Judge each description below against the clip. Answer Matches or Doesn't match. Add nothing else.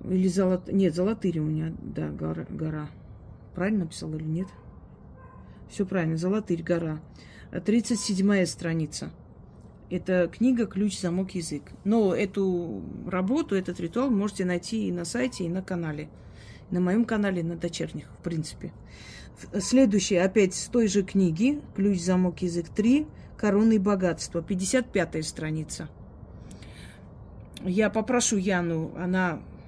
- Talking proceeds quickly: Doesn't match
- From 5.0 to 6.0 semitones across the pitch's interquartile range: Doesn't match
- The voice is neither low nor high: Matches